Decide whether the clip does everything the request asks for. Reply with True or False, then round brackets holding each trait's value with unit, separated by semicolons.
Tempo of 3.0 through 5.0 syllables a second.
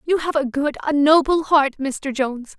True (4.9 syllables/s)